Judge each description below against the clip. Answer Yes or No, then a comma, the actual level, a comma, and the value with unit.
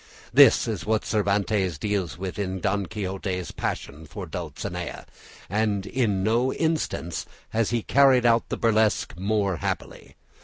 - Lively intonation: No, average, 3.3 semitones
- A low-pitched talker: Yes, low, 105 Hz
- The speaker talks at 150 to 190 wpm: No, average, 140 wpm